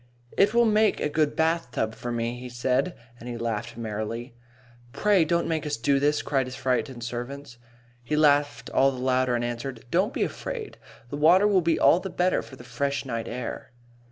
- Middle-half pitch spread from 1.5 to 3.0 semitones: No, average, 5.1 semitones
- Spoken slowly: No, average, 195 wpm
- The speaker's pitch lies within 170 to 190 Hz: No, low, 135 Hz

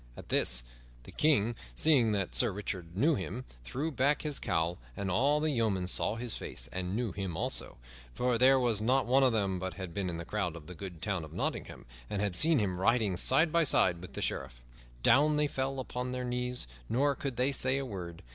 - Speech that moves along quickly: Yes, fast, 220 wpm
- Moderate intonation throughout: No, wide, 6.2 semitones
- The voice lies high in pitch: No, low, 115 Hz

